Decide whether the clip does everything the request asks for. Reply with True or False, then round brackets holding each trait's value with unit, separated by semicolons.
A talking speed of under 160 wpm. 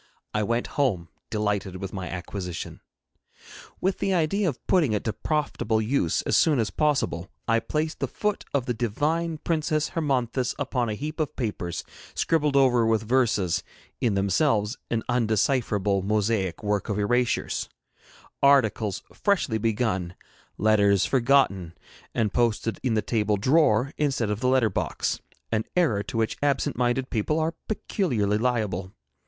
True (150 wpm)